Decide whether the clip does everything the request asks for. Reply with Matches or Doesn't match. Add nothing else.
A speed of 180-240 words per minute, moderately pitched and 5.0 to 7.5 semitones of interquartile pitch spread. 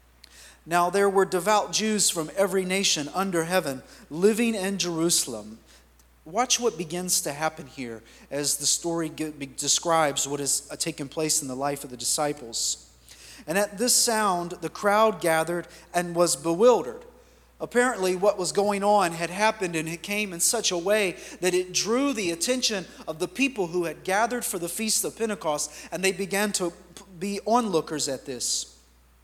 Doesn't match